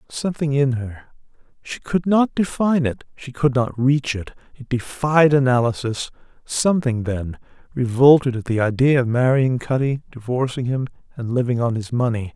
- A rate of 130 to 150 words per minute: Yes, average, 145 wpm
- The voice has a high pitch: No, low, 130 Hz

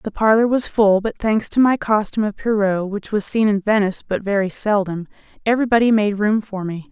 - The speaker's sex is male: No, female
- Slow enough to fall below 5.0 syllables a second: No, 5.6 syllables/s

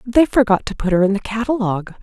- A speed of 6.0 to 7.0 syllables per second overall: Yes, 6.4 syllables/s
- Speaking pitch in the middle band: No, high, 215 Hz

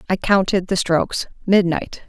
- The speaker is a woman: Yes, female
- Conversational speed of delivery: No, slow, 115 wpm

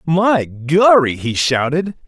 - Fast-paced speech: No, slow, 115 wpm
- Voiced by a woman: No, male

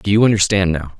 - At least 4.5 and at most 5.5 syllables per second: No, 6.7 syllables/s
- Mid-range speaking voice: No, very low, 95 Hz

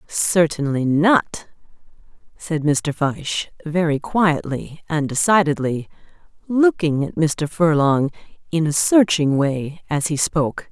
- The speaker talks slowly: Yes, slow, 110 wpm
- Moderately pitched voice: Yes, medium, 160 Hz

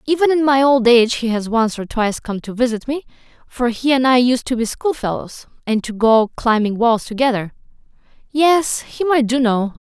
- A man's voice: No, female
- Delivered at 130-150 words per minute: No, average, 200 wpm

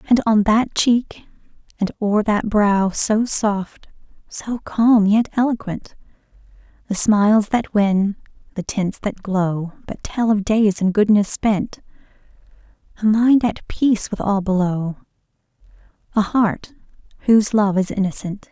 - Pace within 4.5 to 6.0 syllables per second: No, 4.0 syllables/s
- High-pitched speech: Yes, high, 210 Hz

